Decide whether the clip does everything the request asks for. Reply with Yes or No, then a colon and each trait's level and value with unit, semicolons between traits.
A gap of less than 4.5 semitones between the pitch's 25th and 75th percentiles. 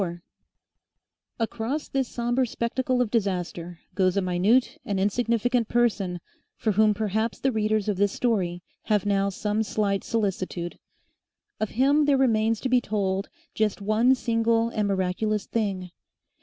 Yes: average, 3.2 semitones